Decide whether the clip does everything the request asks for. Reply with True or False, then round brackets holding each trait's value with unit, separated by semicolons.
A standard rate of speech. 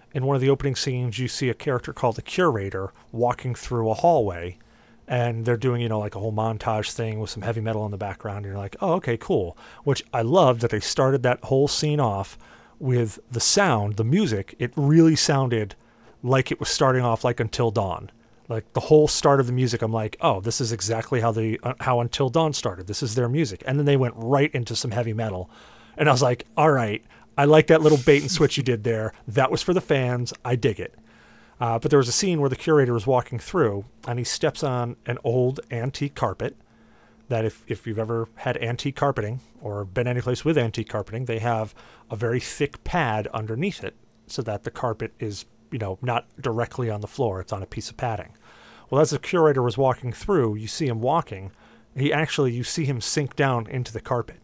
False (225 wpm)